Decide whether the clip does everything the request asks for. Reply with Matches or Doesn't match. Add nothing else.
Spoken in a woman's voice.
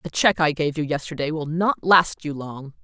Matches